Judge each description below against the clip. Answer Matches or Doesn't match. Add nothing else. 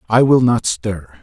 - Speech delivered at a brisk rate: Doesn't match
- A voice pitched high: Doesn't match